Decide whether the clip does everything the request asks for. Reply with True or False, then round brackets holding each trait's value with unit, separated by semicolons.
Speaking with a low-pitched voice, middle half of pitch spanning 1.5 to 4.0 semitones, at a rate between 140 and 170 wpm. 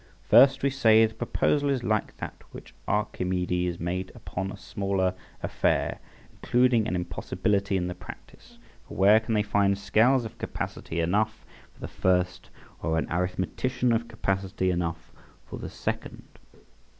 True (100 Hz; 3.7 semitones; 150 wpm)